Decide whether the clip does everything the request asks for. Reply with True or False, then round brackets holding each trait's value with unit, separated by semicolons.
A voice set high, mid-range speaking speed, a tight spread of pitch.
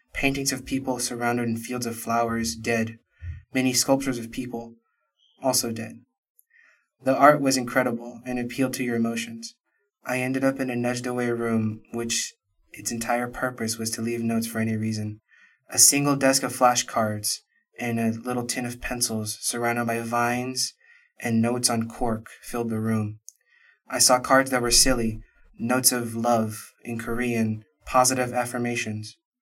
False (120 Hz; 155 wpm; 1.9 semitones)